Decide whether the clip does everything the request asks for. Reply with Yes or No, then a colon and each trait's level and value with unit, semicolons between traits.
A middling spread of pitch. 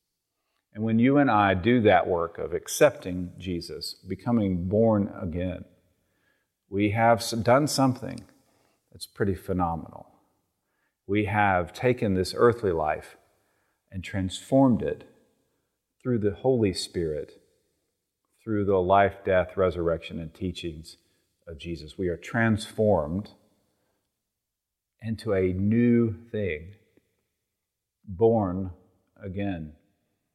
Yes: average, 3.8 semitones